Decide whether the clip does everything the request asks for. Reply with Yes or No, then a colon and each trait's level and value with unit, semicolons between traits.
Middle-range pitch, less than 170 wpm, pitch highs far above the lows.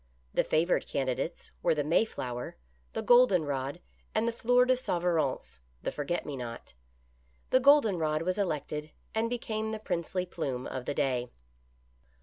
Yes: medium, 170 Hz; average, 150 wpm; wide, 7.7 semitones